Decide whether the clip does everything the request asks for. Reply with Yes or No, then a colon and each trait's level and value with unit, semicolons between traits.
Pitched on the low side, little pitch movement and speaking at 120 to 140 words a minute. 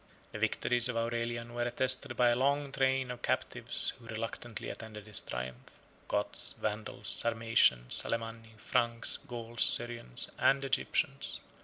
Yes: low, 115 Hz; narrow, 1.7 semitones; slow, 135 wpm